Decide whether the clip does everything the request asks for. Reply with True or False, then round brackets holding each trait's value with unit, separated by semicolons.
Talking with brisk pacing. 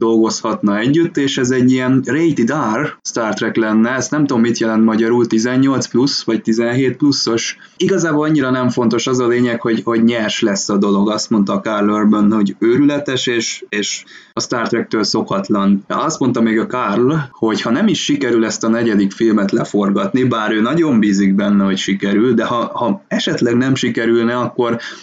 True (185 wpm)